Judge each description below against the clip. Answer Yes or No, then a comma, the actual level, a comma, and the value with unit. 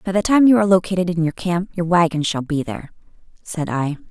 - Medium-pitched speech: Yes, medium, 175 Hz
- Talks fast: Yes, fast, 235 wpm